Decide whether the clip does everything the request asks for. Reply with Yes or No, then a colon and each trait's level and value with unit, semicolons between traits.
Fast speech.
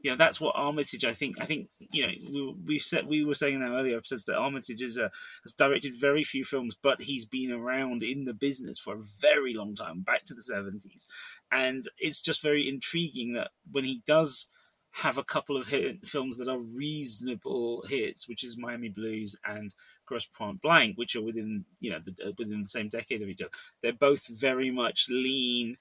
Yes: fast, 210 wpm